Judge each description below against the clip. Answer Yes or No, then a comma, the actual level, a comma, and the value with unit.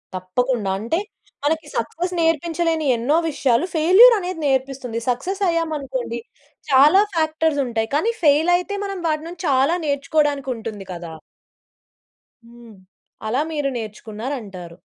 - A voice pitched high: Yes, very high, 280 Hz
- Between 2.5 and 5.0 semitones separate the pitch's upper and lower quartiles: No, wide, 5.6 semitones